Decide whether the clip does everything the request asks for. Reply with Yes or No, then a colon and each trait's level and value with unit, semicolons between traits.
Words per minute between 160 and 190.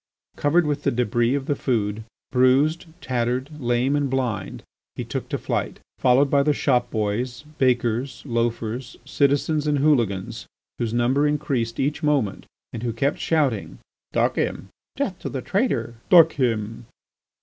No: average, 150 wpm